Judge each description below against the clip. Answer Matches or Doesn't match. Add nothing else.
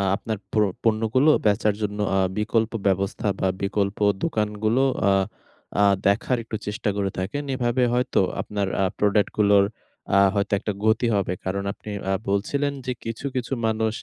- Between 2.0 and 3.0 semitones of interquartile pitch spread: Matches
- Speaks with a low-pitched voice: Matches